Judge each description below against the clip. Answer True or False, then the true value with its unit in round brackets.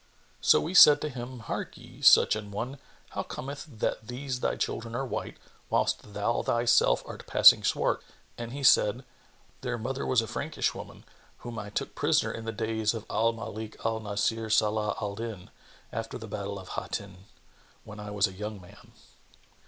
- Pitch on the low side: True (115 Hz)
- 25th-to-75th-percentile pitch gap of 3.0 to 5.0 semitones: False (2.5 semitones)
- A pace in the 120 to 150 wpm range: False (180 wpm)